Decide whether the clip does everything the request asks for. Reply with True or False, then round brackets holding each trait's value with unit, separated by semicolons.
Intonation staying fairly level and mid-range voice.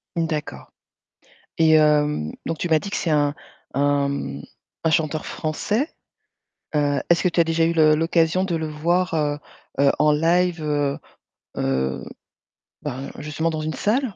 True (2.2 semitones; 155 Hz)